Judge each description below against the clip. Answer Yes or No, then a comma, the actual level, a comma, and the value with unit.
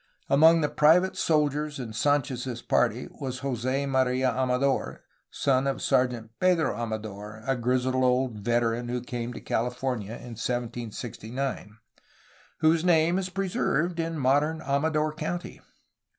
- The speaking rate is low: Yes, slow, 130 wpm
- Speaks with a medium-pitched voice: No, low, 130 Hz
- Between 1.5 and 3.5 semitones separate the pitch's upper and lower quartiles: No, average, 4.0 semitones